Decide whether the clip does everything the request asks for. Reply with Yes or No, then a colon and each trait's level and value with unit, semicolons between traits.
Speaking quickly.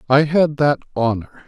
No: average, 160 wpm